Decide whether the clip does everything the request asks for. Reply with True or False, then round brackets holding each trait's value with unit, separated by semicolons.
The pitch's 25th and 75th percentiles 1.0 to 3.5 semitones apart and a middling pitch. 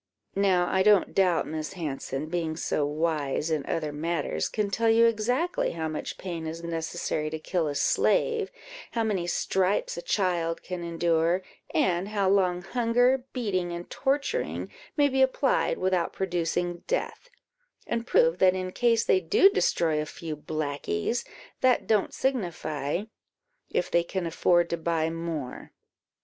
False (4.9 semitones; 175 Hz)